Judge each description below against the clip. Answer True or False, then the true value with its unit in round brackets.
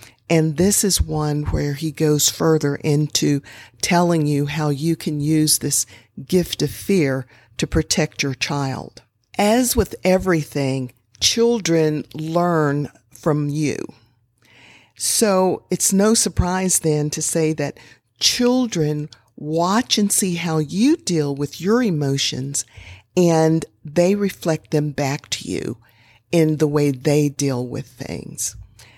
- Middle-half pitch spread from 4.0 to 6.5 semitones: True (4.3 semitones)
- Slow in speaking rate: True (130 wpm)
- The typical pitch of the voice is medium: True (150 Hz)